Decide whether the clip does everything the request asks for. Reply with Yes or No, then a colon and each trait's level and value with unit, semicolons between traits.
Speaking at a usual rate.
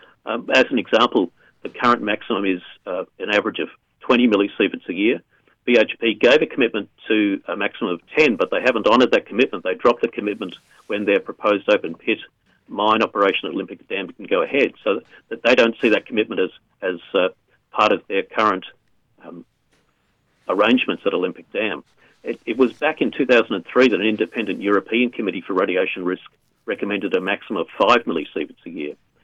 Yes: average, 185 wpm